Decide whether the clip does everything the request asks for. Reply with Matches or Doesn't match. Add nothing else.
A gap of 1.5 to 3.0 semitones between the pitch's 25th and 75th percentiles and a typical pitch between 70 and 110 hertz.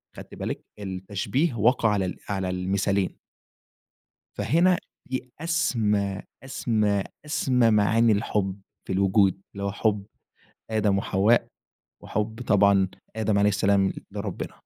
Matches